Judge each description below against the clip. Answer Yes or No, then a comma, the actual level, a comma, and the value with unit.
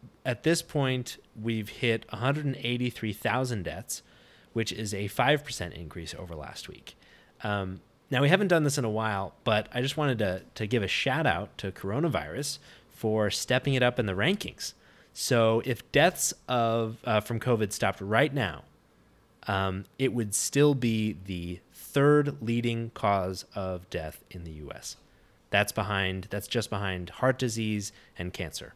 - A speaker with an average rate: Yes, average, 160 wpm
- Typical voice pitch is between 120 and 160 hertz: No, low, 110 Hz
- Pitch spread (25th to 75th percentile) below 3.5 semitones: No, average, 4.6 semitones